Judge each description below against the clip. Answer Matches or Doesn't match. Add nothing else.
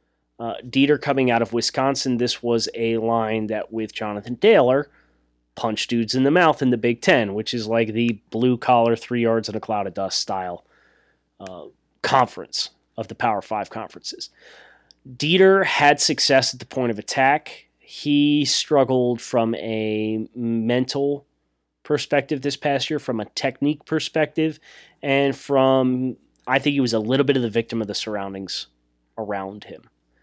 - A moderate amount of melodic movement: Matches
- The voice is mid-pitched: Doesn't match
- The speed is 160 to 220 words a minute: Matches